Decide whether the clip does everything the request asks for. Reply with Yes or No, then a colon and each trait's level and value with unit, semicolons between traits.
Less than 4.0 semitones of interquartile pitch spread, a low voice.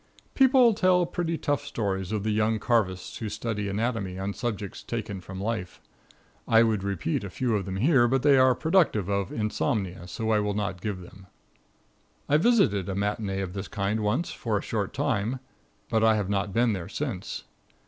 Yes: average, 3.6 semitones; low, 105 Hz